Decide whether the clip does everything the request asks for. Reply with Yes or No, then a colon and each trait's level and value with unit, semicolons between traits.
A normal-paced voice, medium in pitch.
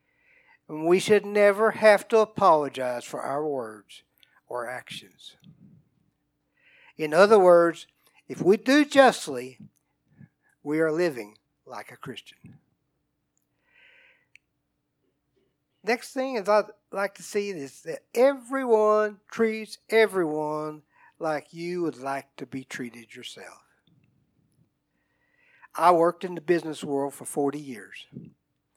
No: slow, 110 wpm; medium, 175 Hz